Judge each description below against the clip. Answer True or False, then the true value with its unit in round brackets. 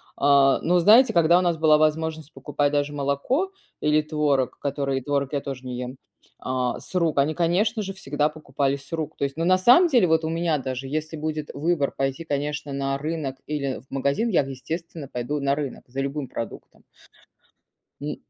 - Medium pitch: True (150 Hz)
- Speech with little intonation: False (3.0 semitones)